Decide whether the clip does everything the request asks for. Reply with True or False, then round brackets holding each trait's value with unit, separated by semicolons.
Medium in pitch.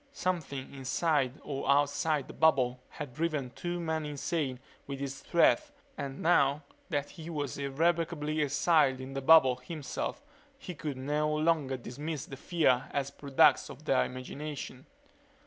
True (145 Hz)